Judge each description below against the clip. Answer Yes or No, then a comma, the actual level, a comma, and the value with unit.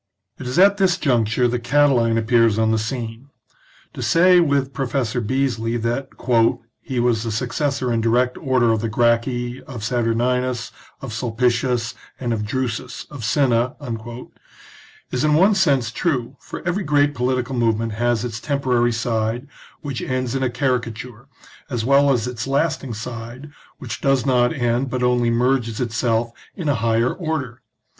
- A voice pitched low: Yes, low, 125 Hz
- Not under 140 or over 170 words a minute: Yes, average, 160 wpm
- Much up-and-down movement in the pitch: No, average, 2.7 semitones